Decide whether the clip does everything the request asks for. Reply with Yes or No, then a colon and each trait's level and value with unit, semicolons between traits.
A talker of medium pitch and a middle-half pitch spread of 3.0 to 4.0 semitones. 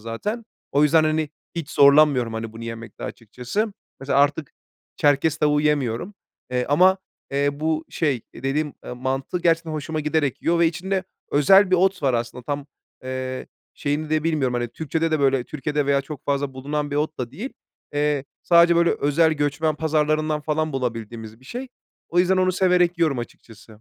Yes: medium, 150 Hz; average, 3.5 semitones